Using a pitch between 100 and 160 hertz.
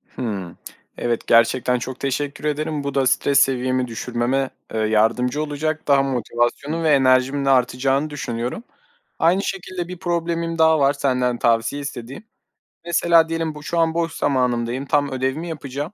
Yes: low, 135 Hz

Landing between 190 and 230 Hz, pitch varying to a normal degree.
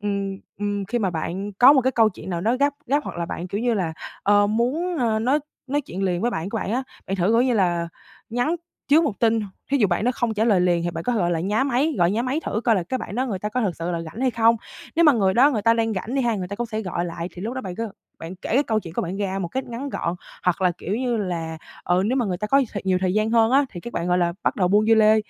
Yes: high, 215 Hz; average, 4.9 semitones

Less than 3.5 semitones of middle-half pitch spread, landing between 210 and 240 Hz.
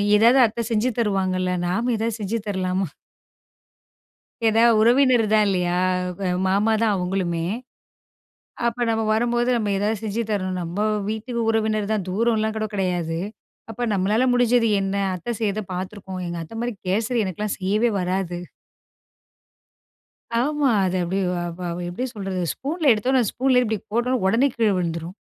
No: average, 3.8 semitones; high, 215 Hz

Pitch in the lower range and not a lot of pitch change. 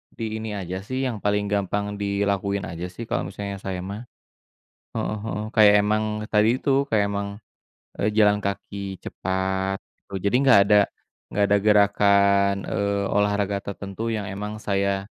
Yes: low, 100 Hz; narrow, 1.0 semitones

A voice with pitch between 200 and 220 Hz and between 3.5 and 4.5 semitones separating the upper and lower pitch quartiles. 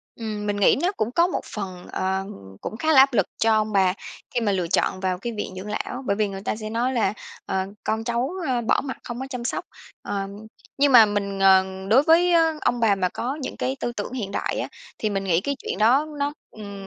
Yes: high, 215 Hz; average, 4.2 semitones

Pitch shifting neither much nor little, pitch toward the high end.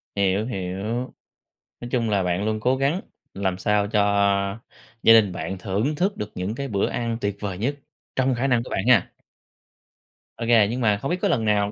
No: average, 3.9 semitones; low, 110 Hz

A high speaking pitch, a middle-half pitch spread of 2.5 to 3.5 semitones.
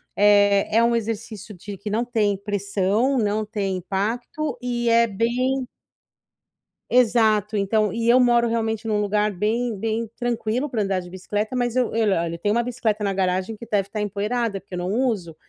Yes: high, 215 Hz; average, 2.8 semitones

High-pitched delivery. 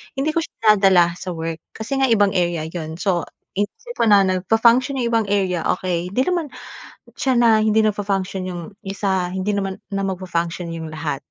Yes: high, 195 Hz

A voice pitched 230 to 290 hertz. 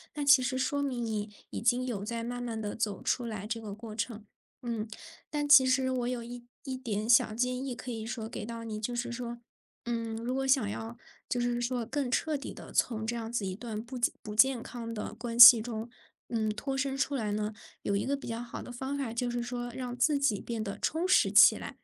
Yes: high, 240 Hz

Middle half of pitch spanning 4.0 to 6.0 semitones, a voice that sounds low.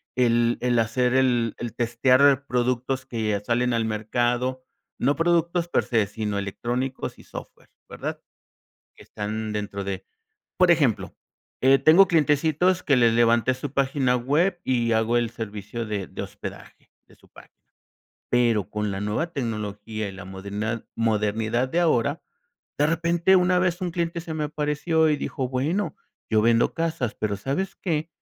Yes: average, 5.3 semitones; low, 125 Hz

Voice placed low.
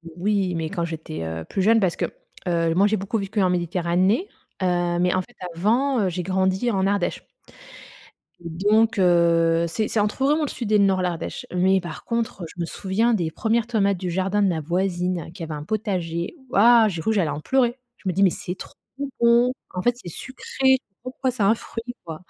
No: high, 190 Hz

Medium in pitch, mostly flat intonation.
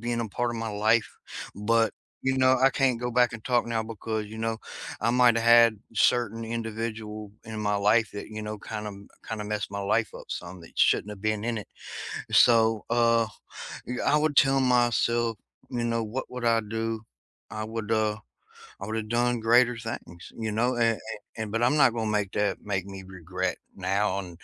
No: low, 115 Hz; narrow, 1.9 semitones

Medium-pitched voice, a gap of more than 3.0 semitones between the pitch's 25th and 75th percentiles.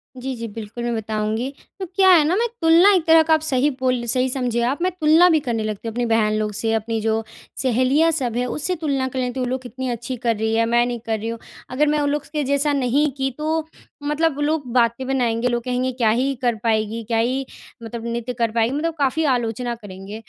No: very high, 250 Hz; average, 4.2 semitones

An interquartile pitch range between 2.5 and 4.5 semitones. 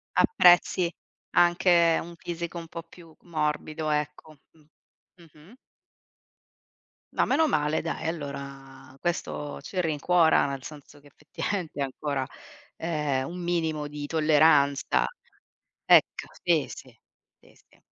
Yes: average, 2.8 semitones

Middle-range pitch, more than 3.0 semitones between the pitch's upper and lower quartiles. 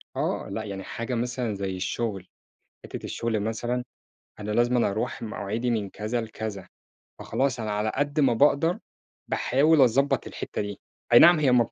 No: low, 115 Hz; average, 3.4 semitones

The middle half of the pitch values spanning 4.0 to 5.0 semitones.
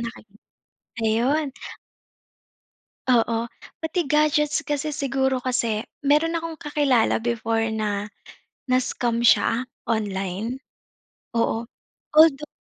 Yes: average, 4.7 semitones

